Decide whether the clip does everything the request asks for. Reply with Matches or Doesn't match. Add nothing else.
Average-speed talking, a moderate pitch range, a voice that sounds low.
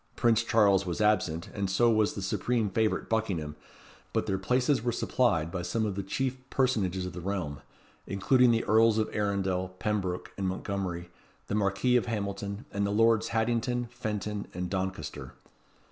Matches